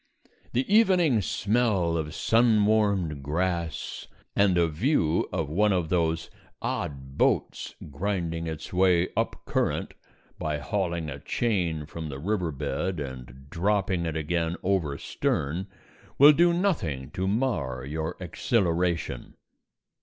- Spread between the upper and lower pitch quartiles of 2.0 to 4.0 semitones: No, average, 4.8 semitones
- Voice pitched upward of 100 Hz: No, very low, 85 Hz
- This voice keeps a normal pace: No, slow, 125 wpm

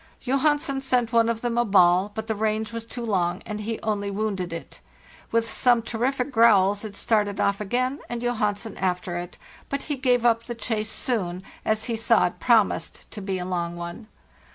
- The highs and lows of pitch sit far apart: No, average, 3.3 semitones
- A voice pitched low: No, high, 220 Hz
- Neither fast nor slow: Yes, average, 195 wpm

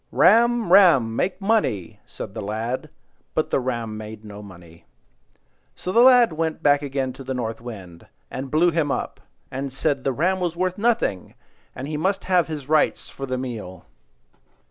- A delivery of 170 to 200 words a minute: Yes, average, 175 wpm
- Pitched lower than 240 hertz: Yes, low, 135 Hz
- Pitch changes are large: Yes, wide, 7.7 semitones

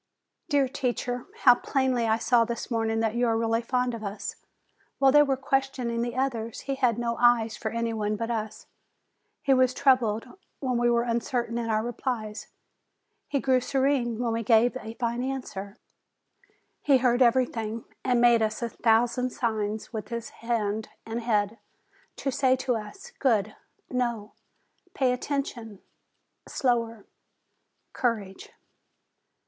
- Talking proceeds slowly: No, average, 150 wpm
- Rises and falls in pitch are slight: Yes, narrow, 2.2 semitones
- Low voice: No, high, 235 Hz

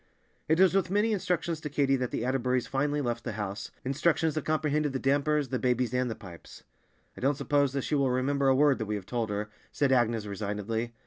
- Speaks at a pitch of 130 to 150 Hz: Yes, low, 135 Hz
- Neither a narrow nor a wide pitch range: Yes, average, 3.9 semitones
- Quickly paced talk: Yes, fast, 220 wpm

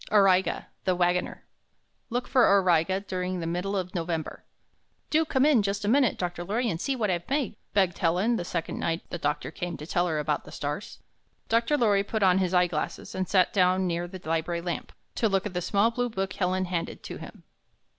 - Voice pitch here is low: No, medium, 185 Hz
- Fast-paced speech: Yes, fast, 215 wpm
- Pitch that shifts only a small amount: No, average, 3.0 semitones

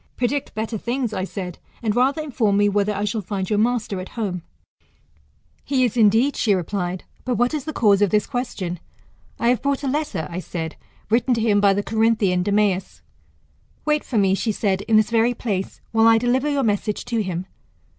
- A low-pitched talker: No, high, 215 Hz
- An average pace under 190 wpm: No, average, 200 wpm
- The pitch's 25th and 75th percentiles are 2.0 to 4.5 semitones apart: Yes, average, 3.7 semitones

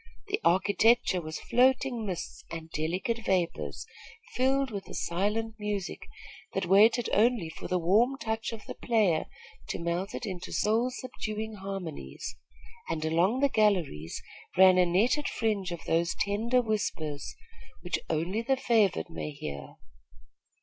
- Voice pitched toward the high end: Yes, high, 200 Hz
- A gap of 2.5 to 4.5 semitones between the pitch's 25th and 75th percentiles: No, average, 5.1 semitones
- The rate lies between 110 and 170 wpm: Yes, average, 140 wpm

